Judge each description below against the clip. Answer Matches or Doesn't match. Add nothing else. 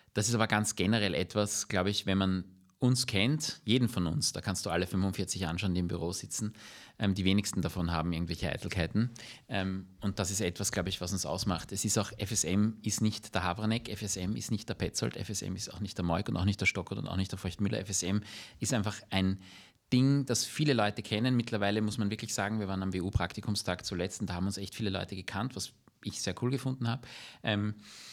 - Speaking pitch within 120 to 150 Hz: Doesn't match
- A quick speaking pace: Matches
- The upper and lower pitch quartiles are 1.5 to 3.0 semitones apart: Matches